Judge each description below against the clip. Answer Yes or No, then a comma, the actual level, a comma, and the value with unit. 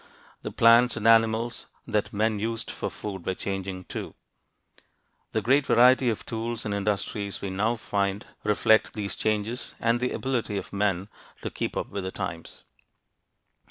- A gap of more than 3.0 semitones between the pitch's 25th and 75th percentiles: No, narrow, 2.4 semitones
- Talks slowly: No, average, 160 wpm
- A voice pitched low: Yes, low, 110 Hz